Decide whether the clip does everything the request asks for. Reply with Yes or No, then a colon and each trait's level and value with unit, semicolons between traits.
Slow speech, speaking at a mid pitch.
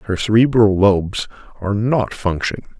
No: slow, 130 wpm; low, 105 Hz